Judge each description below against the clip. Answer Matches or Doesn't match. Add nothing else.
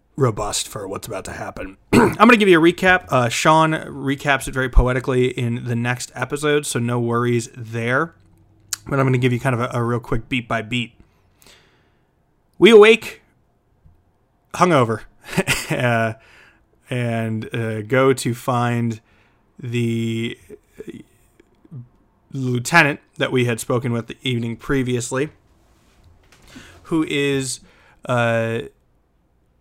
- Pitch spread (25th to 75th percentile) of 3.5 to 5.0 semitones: Doesn't match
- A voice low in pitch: Matches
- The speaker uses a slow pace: Matches